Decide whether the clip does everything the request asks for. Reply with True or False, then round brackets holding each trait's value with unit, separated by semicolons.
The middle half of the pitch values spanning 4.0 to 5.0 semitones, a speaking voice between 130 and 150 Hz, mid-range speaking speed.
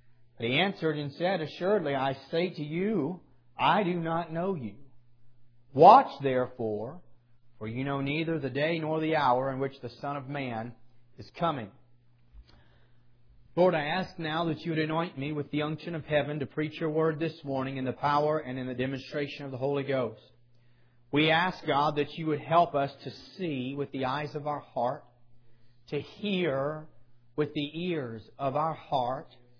True (4.5 semitones; 140 Hz; 180 wpm)